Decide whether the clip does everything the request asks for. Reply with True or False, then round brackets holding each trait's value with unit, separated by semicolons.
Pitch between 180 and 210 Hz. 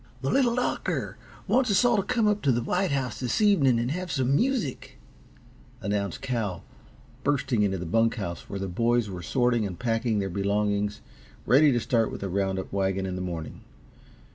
False (115 Hz)